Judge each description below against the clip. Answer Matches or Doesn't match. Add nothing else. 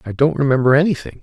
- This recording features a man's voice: Matches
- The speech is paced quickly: Doesn't match